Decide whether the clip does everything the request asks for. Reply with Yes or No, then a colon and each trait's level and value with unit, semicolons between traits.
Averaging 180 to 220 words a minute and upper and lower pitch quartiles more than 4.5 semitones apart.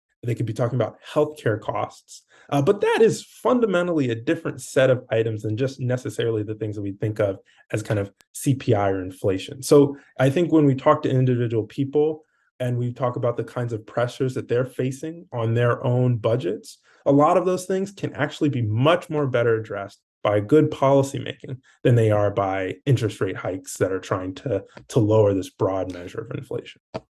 Yes: average, 200 wpm; average, 4.9 semitones